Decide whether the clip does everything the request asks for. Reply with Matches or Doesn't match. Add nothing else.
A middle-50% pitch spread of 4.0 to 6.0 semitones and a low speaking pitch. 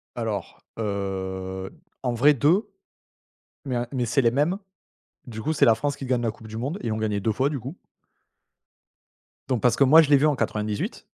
Matches